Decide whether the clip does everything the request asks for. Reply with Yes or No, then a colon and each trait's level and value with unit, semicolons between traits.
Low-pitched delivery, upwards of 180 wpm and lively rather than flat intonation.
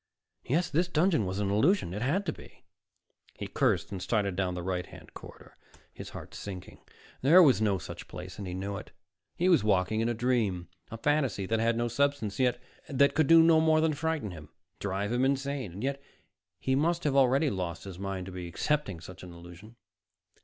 Yes: low, 115 Hz; average, 200 wpm; wide, 7.2 semitones